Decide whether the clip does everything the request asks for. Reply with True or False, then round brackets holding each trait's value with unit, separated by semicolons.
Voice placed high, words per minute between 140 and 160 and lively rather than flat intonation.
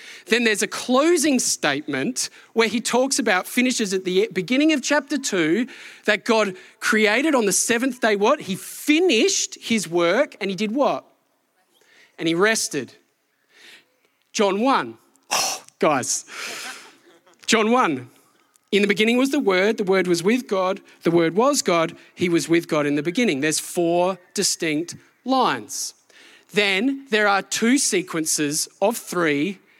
True (215 Hz; 150 wpm; 5.7 semitones)